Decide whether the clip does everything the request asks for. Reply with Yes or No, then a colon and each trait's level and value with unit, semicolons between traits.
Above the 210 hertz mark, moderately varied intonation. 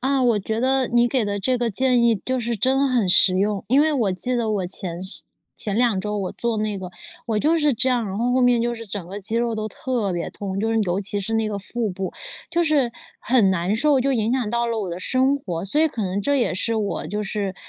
Yes: high, 225 Hz; average, 4.0 semitones